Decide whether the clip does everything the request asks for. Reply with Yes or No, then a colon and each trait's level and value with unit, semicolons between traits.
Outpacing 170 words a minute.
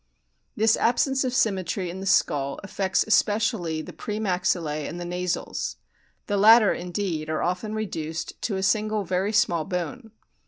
No: average, 155 wpm